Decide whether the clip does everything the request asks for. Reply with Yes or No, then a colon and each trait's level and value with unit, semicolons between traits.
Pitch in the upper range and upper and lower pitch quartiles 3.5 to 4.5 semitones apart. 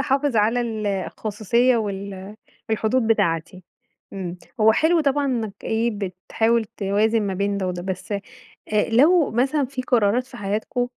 Yes: high, 220 Hz; average, 3.8 semitones